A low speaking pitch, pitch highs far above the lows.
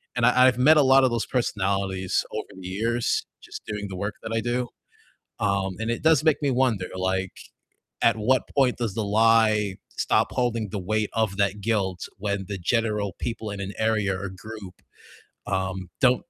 No: low, 105 Hz; average, 3.5 semitones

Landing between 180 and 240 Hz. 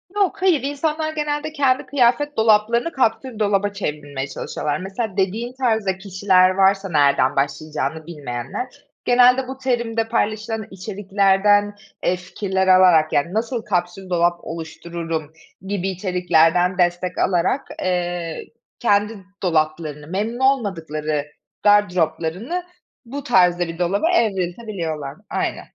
Yes: high, 190 Hz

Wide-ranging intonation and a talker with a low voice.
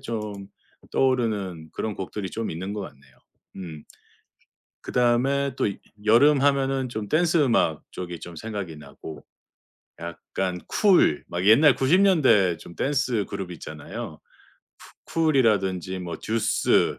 Yes: wide, 6.8 semitones; low, 105 Hz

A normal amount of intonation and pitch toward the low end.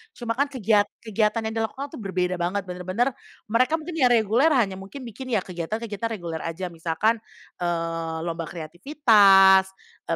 No: average, 4.7 semitones; high, 205 Hz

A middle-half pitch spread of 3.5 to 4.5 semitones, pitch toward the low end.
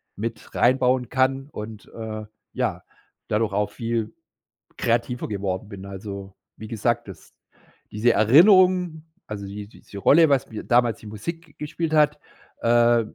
Yes: average, 4.1 semitones; low, 115 Hz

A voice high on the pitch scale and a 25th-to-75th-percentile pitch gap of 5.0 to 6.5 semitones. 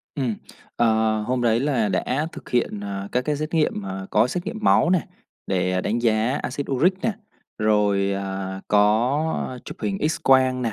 No: low, 115 Hz; average, 5.3 semitones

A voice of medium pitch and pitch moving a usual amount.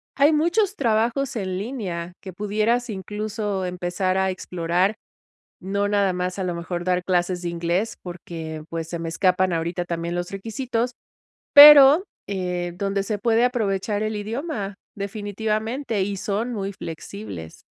No: high, 195 Hz; average, 3.9 semitones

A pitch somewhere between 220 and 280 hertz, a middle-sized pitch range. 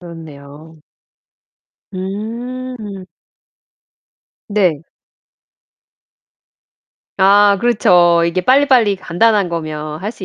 No: high, 190 Hz; average, 4.5 semitones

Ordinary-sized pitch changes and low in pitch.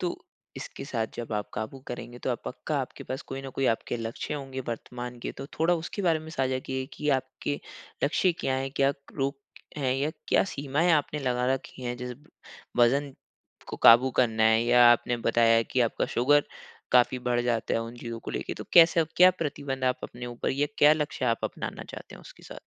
Yes: average, 3.1 semitones; low, 130 Hz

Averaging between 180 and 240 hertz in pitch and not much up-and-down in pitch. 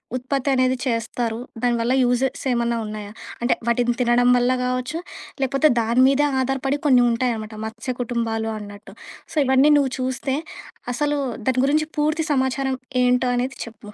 No: very high, 250 Hz; narrow, 2.2 semitones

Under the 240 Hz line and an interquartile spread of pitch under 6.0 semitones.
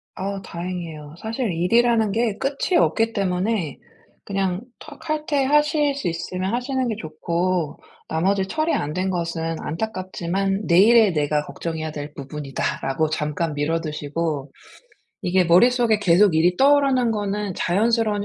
Yes: medium, 185 Hz; wide, 5.6 semitones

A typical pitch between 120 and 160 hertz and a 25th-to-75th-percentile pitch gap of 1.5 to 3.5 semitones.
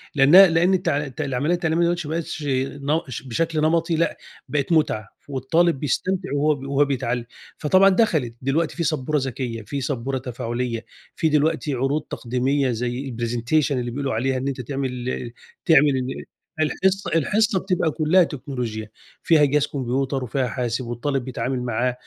No: medium, 140 Hz; average, 4.1 semitones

